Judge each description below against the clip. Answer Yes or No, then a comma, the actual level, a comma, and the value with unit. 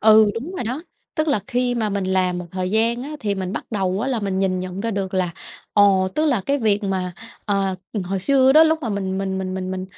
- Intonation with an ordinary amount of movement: Yes, average, 4.3 semitones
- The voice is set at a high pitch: Yes, high, 200 Hz